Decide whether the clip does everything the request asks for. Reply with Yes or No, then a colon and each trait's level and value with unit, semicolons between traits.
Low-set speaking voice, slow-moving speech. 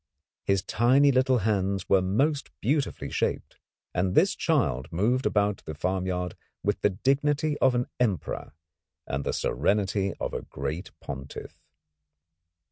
Yes: low, 100 Hz; slow, 130 wpm